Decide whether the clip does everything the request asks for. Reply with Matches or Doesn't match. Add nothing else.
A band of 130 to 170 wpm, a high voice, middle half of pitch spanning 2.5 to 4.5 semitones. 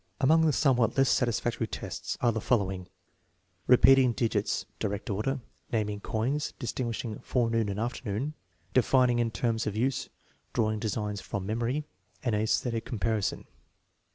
Doesn't match